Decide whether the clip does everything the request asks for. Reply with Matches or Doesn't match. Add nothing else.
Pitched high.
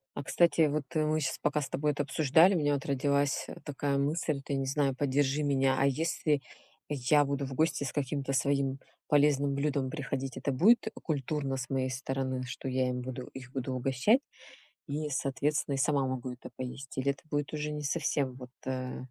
Doesn't match